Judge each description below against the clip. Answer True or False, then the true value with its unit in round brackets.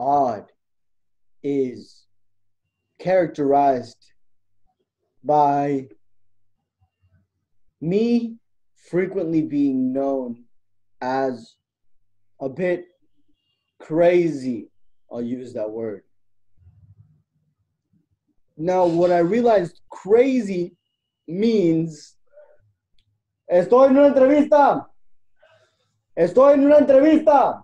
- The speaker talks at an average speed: False (65 wpm)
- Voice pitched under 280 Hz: True (135 Hz)